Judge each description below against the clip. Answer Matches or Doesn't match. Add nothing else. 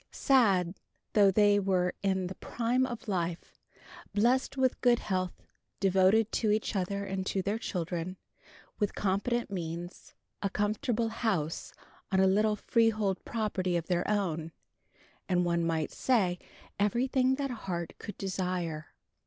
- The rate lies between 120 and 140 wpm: Matches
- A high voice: Matches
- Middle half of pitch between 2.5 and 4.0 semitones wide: Matches